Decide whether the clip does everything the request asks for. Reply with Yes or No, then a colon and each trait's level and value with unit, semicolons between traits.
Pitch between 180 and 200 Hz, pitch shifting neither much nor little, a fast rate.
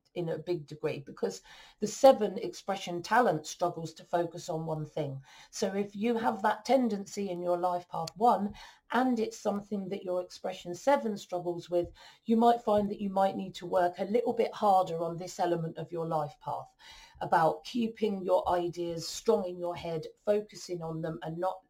No: medium, 185 Hz; average, 3.6 semitones; average, 190 wpm